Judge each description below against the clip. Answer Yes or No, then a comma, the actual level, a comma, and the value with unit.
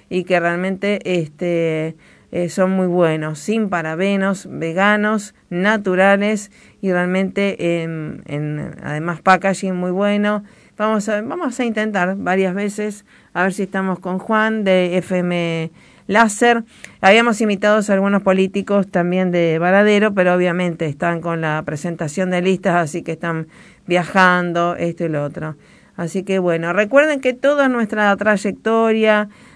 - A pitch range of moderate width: Yes, average, 3.2 semitones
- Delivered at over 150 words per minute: No, average, 140 wpm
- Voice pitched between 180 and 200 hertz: Yes, high, 190 Hz